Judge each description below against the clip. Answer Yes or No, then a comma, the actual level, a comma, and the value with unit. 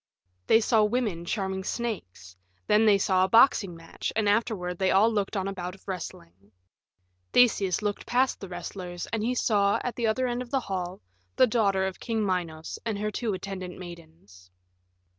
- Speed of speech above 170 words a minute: Yes, average, 180 wpm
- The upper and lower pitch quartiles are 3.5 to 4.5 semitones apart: Yes, average, 3.8 semitones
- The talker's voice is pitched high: Yes, high, 195 Hz